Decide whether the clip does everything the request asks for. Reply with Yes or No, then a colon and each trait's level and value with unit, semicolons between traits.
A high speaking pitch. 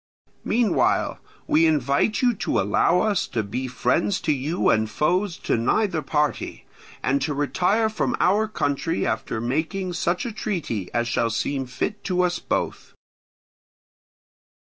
No: medium, 160 Hz